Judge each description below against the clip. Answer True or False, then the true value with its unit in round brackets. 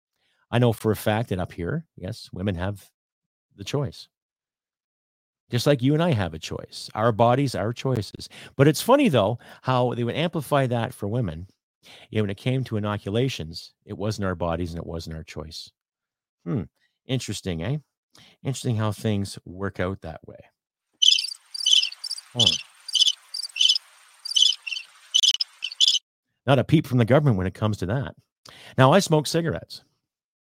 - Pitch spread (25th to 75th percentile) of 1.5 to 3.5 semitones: False (5.3 semitones)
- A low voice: True (115 Hz)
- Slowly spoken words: False (155 wpm)